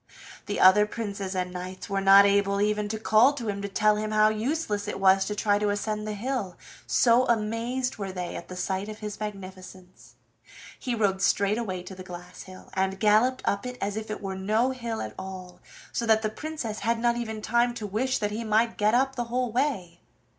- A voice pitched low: No, high, 210 Hz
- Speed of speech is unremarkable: No, fast, 210 wpm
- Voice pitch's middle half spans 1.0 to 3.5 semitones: Yes, average, 3.0 semitones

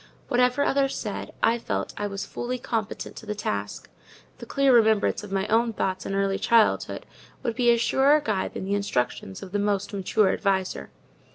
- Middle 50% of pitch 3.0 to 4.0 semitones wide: Yes, average, 3.5 semitones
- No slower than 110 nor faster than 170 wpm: No, average, 185 wpm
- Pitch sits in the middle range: No, high, 210 Hz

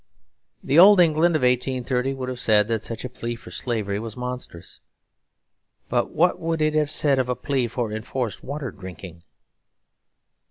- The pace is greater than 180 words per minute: No, average, 165 wpm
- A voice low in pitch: Yes, low, 125 Hz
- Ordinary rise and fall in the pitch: Yes, average, 4.4 semitones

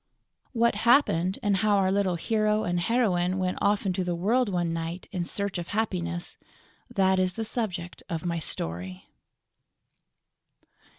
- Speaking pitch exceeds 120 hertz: Yes, medium, 185 Hz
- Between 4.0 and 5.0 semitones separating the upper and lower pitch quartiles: No, average, 3.4 semitones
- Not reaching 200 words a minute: Yes, average, 145 wpm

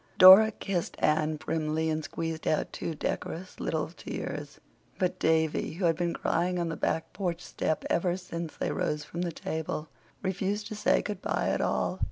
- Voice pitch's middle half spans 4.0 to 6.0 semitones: No, narrow, 2.6 semitones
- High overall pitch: No, medium, 165 Hz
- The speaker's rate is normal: Yes, average, 180 wpm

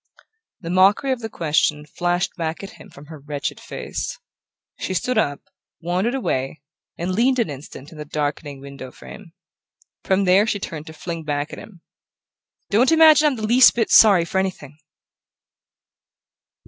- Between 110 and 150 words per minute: No, average, 160 wpm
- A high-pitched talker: No, medium, 175 Hz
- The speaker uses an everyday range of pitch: No, wide, 6.3 semitones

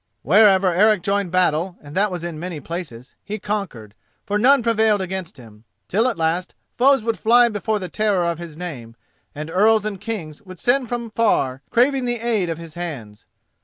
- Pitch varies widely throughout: No, average, 4.9 semitones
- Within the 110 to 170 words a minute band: No, average, 190 wpm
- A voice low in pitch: No, high, 190 Hz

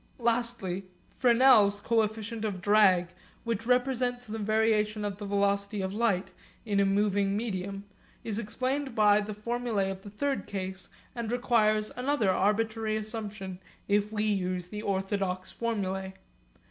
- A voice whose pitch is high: Yes, high, 210 Hz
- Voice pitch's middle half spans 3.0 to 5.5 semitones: No, narrow, 2.5 semitones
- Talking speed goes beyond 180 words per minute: No, slow, 135 wpm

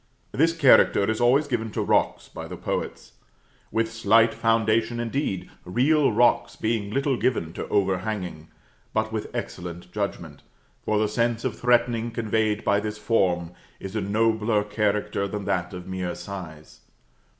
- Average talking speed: Yes, average, 150 wpm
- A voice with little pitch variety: No, average, 3.0 semitones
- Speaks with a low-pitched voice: Yes, low, 110 Hz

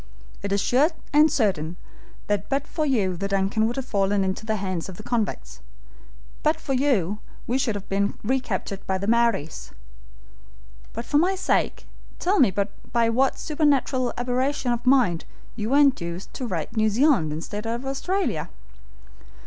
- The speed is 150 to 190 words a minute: Yes, average, 165 wpm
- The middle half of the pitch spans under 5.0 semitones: No, wide, 5.5 semitones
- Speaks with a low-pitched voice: No, high, 230 Hz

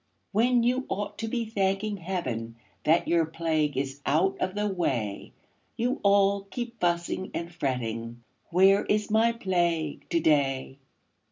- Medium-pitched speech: Yes, medium, 175 Hz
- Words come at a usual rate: Yes, average, 145 wpm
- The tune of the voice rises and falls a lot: Yes, wide, 5.9 semitones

